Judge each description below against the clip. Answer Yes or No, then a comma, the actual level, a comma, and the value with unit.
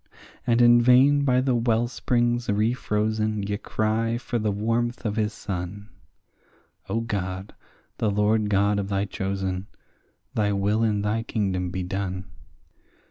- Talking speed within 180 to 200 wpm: No, slow, 135 wpm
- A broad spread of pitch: No, average, 2.7 semitones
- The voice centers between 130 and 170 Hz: No, low, 105 Hz